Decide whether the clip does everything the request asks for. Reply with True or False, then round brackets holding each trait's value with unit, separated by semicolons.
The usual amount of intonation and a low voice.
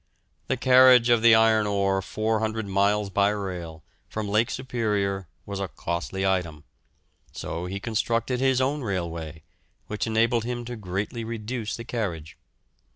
True (3.3 semitones; 105 Hz)